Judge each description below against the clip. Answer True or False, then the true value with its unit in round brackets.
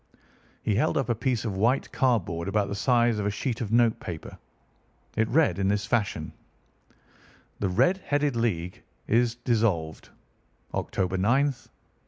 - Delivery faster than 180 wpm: False (155 wpm)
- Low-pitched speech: True (110 Hz)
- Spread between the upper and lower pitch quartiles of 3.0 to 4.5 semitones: True (3.7 semitones)